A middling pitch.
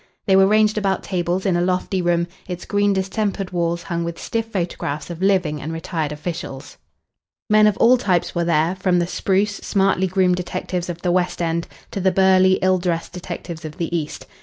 Yes: medium, 180 Hz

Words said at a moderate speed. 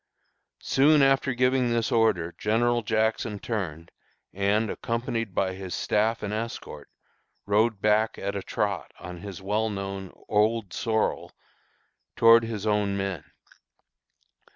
No: slow, 125 wpm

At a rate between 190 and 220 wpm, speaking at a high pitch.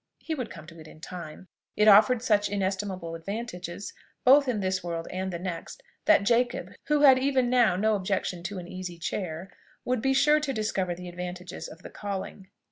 Yes: average, 195 wpm; high, 195 Hz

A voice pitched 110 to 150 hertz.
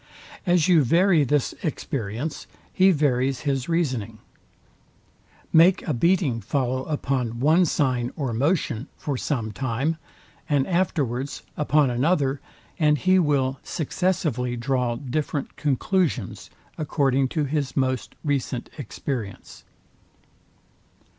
Yes: medium, 140 Hz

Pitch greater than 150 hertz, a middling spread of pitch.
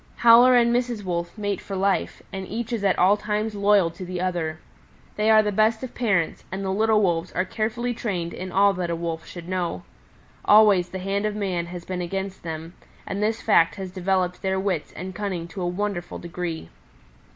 Yes: high, 190 Hz; average, 3.1 semitones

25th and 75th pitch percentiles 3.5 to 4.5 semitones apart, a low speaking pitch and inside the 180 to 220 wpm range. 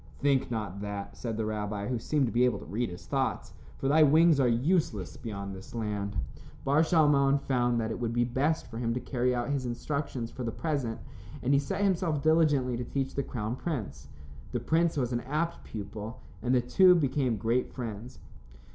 Yes: average, 4.1 semitones; low, 125 Hz; average, 200 wpm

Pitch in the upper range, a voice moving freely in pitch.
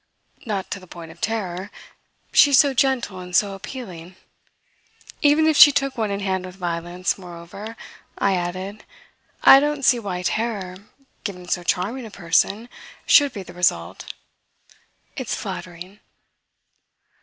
No: high, 195 Hz; average, 4.5 semitones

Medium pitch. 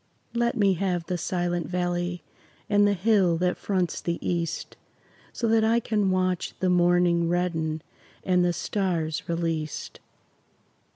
Yes: medium, 180 Hz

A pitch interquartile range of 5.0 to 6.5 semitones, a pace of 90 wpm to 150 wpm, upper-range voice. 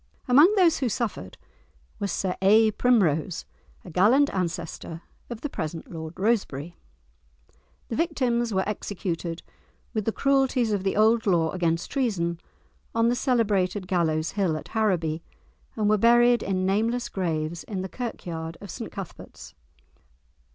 Yes: wide, 5.5 semitones; average, 140 wpm; high, 200 Hz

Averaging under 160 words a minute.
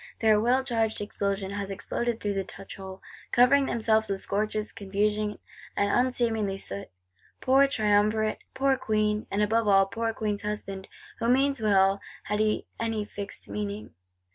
Yes: average, 150 wpm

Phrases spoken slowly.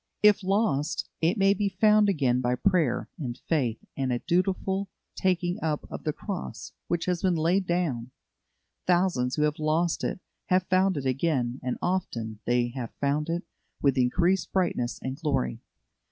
No: average, 165 wpm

